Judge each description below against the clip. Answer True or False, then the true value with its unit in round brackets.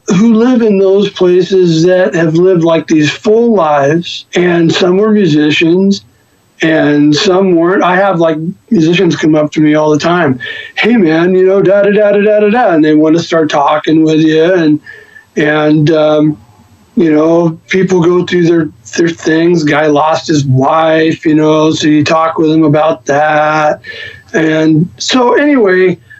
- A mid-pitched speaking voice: True (165 Hz)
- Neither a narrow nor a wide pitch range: True (3.5 semitones)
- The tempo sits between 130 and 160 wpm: False (170 wpm)